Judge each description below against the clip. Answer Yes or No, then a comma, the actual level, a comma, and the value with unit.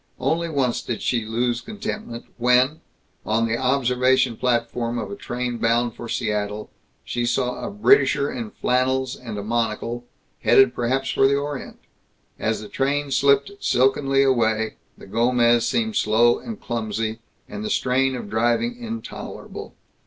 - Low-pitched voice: Yes, low, 125 Hz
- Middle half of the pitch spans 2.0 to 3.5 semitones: Yes, average, 2.7 semitones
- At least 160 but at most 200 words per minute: No, average, 145 wpm